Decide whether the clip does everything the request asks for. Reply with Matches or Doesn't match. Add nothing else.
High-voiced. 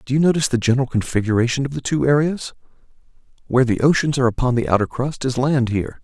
Doesn't match